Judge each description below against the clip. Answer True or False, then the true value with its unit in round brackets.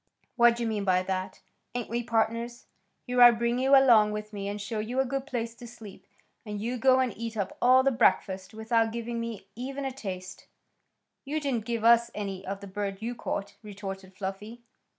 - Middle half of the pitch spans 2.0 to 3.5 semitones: True (3.1 semitones)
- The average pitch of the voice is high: True (230 Hz)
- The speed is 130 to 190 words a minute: False (200 wpm)